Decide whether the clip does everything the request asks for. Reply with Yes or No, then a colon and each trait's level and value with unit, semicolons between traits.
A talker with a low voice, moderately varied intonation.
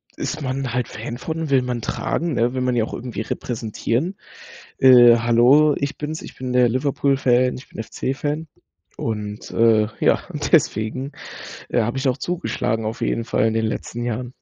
Yes: low, 125 Hz; average, 3.0 semitones